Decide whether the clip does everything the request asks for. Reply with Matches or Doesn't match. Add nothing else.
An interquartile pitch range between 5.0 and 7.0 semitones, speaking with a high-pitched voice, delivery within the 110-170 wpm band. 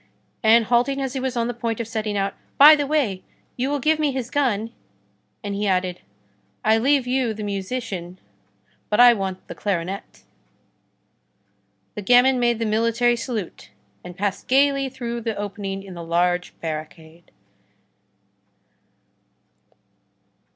Doesn't match